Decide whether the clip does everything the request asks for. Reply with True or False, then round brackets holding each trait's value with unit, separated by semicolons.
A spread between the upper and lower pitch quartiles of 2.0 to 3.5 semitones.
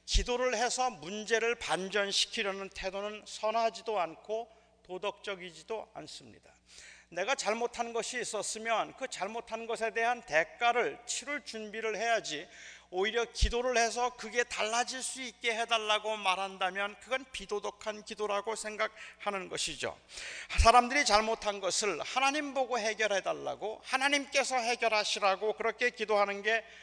True (2.7 semitones)